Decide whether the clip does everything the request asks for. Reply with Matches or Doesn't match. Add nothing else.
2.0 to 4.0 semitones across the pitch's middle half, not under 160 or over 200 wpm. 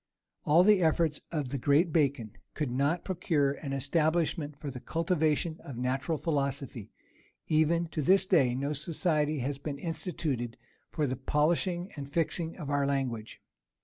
Doesn't match